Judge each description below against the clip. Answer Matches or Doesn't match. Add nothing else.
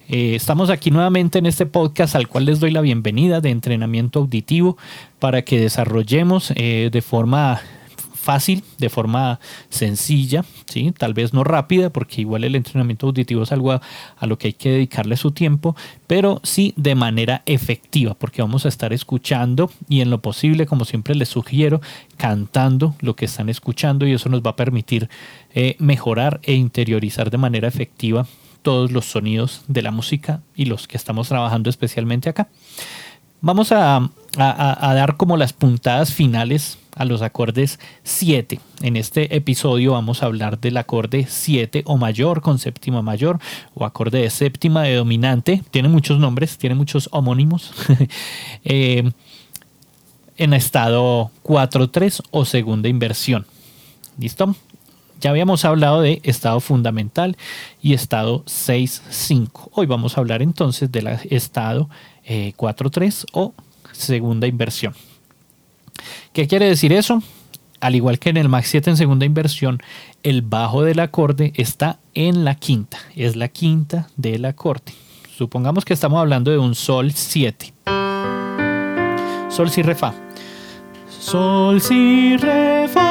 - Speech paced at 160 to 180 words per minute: Doesn't match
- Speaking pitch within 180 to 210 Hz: Doesn't match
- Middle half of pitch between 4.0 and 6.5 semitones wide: Matches